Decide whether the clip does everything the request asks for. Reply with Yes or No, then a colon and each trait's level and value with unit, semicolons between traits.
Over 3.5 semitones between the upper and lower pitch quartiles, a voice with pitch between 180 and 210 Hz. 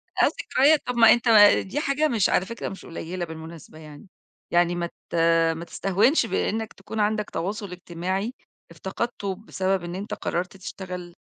Yes: average, 4.2 semitones; high, 190 Hz